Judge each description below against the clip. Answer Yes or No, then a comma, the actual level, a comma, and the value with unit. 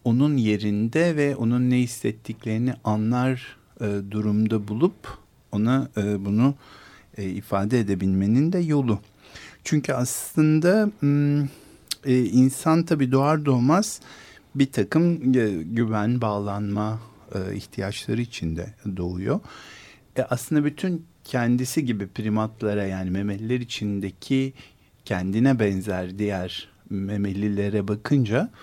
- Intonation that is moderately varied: Yes, average, 4.7 semitones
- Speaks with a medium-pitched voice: No, low, 115 Hz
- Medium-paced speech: Yes, average, 105 wpm